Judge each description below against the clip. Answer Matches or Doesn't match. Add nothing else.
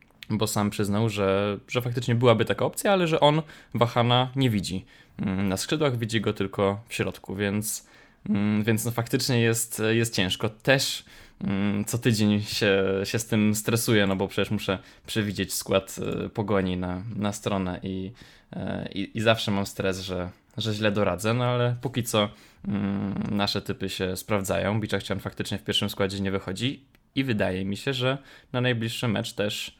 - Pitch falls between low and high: Doesn't match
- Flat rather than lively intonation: Doesn't match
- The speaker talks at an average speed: Doesn't match